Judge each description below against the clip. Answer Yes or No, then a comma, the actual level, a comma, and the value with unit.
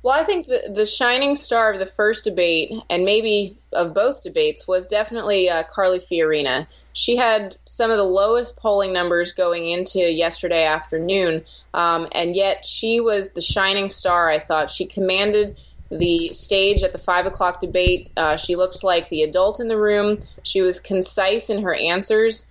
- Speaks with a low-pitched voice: No, high, 190 Hz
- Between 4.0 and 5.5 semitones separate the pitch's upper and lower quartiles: No, average, 3.5 semitones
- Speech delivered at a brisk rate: No, average, 180 wpm